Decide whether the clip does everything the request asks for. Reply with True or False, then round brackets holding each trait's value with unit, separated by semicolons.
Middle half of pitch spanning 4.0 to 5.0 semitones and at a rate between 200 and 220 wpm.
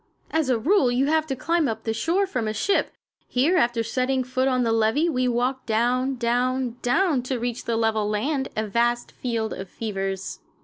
False (2.9 semitones; 205 wpm)